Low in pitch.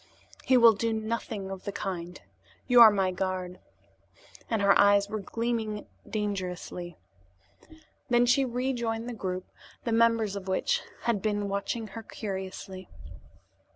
No: high, 210 Hz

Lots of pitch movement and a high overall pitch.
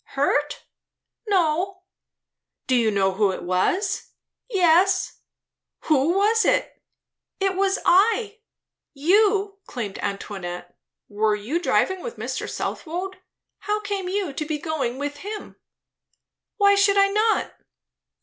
Yes: wide, 7.2 semitones; very high, 360 Hz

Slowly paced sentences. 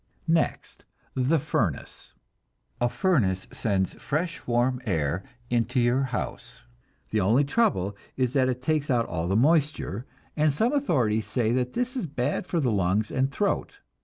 No: average, 155 wpm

